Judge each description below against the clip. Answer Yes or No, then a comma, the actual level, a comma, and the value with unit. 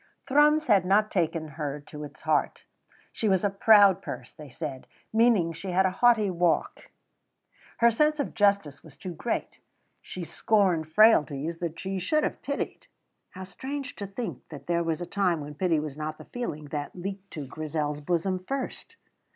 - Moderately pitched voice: Yes, medium, 180 Hz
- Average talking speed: Yes, average, 180 wpm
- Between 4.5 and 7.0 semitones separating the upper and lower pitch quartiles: Yes, average, 5.2 semitones